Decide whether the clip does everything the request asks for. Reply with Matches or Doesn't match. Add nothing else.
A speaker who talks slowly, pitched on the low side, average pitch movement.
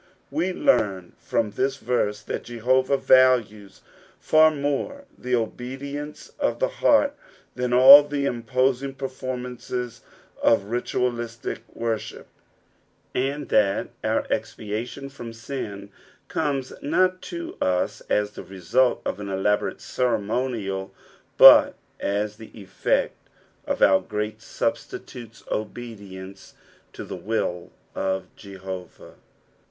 Matches